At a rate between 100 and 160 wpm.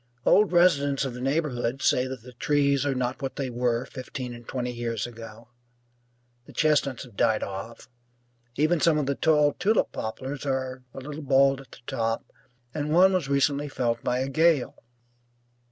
No: average, 175 wpm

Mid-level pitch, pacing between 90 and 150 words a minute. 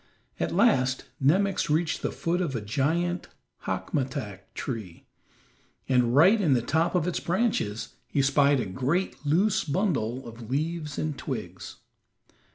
Yes: medium, 145 Hz; average, 140 wpm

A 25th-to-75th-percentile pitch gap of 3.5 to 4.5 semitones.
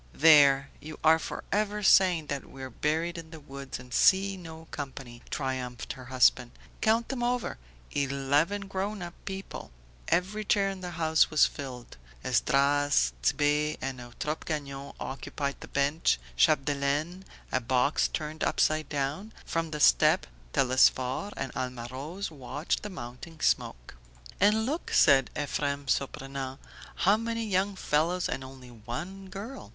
No: wide, 5.5 semitones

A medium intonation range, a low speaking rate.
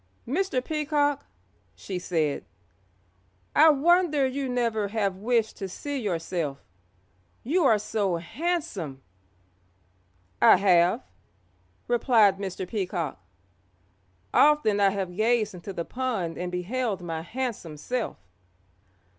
No: wide, 6.5 semitones; slow, 105 wpm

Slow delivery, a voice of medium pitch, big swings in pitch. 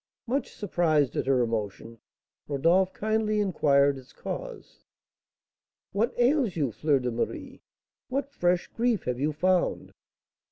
Yes: slow, 125 wpm; medium, 170 Hz; wide, 7.9 semitones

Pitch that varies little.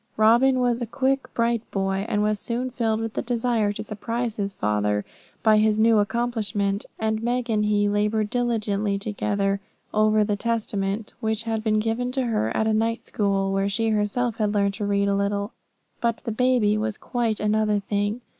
Yes: narrow, 2.2 semitones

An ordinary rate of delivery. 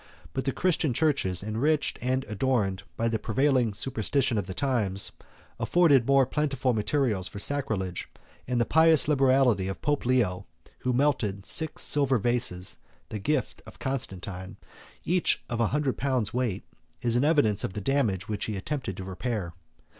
Yes: average, 160 wpm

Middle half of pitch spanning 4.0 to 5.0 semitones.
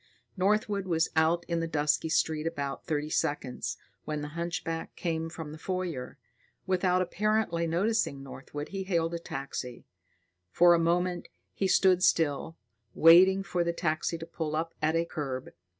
No: average, 2.7 semitones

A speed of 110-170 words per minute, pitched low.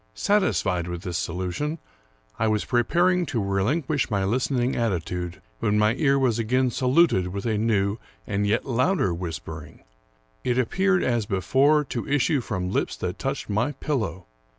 Yes: average, 155 wpm; low, 115 Hz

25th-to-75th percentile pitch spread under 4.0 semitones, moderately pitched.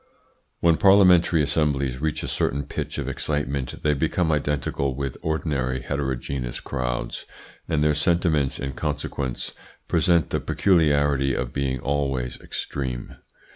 No: average, 2.9 semitones; very low, 70 Hz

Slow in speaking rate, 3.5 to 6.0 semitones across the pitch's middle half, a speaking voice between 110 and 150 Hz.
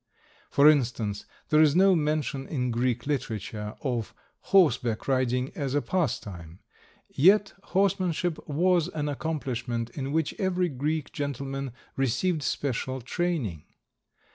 Yes: slow, 115 wpm; average, 4.7 semitones; medium, 140 Hz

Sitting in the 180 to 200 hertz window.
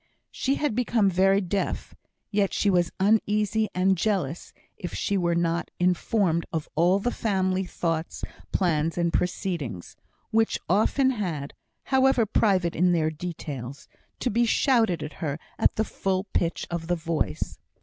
Yes: medium, 185 Hz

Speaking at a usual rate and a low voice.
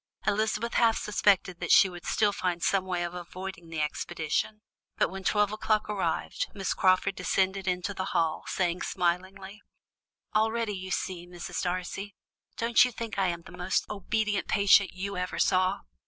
No: average, 170 wpm; high, 190 Hz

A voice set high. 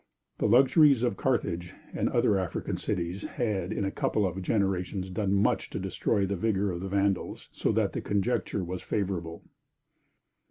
No: low, 100 Hz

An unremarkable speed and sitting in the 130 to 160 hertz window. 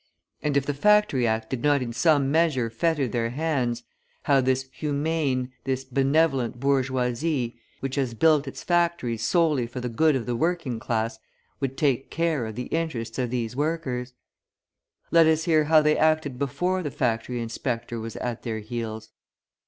Yes: average, 170 wpm; low, 135 Hz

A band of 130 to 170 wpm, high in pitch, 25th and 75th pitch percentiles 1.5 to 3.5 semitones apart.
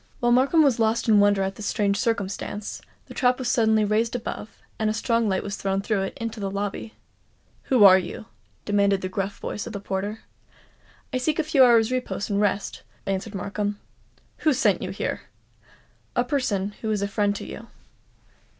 No: average, 190 wpm; high, 210 Hz; average, 2.7 semitones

